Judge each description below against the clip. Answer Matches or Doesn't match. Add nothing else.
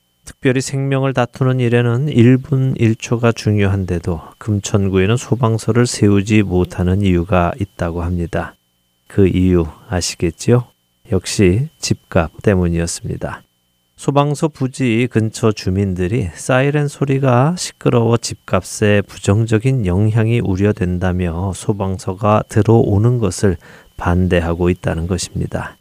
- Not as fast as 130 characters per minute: Doesn't match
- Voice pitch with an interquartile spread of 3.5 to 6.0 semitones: Matches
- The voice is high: Doesn't match